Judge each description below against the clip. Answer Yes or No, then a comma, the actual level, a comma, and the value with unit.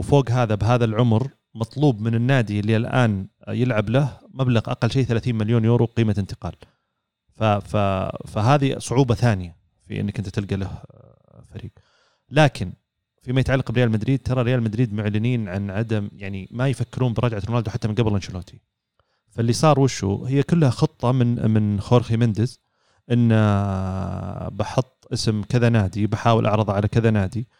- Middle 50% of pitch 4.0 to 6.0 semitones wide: No, average, 3.0 semitones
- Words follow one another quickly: Yes, fast, 150 wpm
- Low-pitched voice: Yes, low, 115 Hz